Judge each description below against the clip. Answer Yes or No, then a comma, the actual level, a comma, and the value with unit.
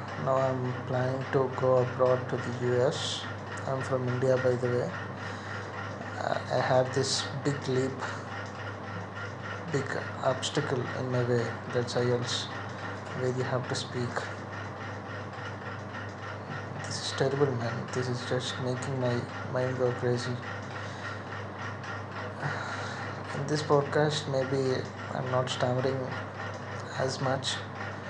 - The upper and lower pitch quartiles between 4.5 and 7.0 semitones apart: No, average, 3.4 semitones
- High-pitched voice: No, low, 120 Hz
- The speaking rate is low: Yes, slow, 115 wpm